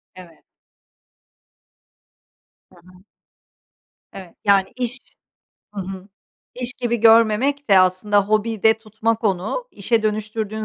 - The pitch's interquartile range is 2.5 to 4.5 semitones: Yes, average, 2.9 semitones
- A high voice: Yes, high, 215 Hz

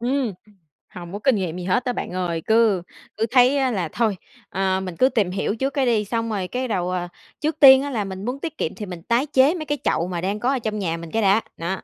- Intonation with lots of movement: Yes, wide, 5.8 semitones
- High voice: Yes, high, 215 Hz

